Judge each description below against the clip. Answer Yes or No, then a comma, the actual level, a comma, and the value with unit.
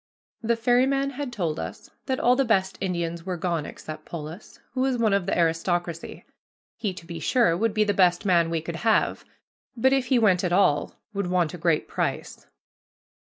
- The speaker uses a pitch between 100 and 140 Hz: No, high, 190 Hz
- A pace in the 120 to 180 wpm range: No, average, 195 wpm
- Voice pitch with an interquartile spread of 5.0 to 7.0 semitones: Yes, wide, 5.5 semitones